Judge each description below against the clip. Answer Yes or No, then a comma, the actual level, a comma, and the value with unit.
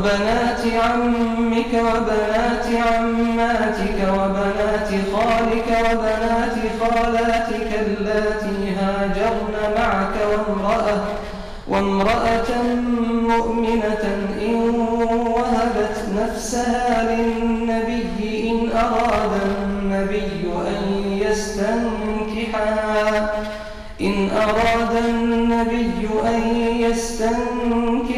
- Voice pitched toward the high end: Yes, high, 225 Hz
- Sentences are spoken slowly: Yes, slow, 60 wpm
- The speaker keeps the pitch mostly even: Yes, narrow, 1.6 semitones